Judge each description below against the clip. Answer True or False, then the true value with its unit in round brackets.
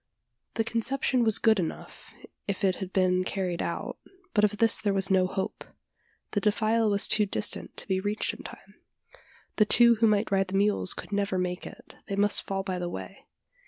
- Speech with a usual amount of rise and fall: False (2.2 semitones)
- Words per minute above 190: True (200 wpm)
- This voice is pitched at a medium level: False (200 Hz)